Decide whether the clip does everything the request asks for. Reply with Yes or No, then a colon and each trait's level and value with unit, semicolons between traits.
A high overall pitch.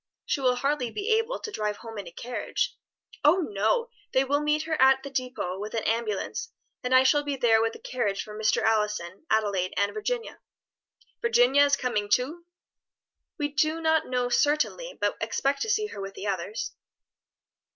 Yes: very high, 255 Hz